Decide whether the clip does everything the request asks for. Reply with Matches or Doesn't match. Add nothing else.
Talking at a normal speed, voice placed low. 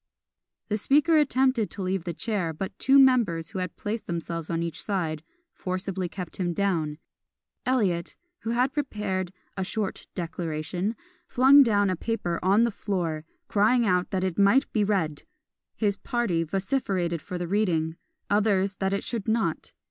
Doesn't match